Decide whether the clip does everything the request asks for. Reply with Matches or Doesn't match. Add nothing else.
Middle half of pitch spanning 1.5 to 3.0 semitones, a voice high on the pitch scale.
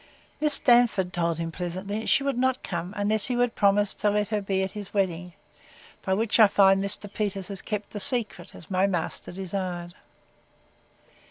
Matches